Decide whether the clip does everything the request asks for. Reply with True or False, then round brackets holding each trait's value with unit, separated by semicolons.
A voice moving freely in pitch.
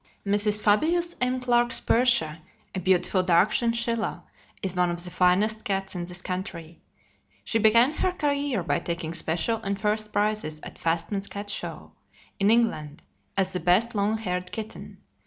False (4.2 semitones)